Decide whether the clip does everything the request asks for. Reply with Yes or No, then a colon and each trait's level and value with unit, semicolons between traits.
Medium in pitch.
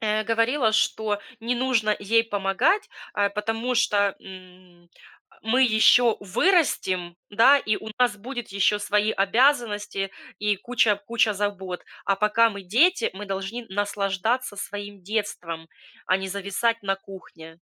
No: high, 210 Hz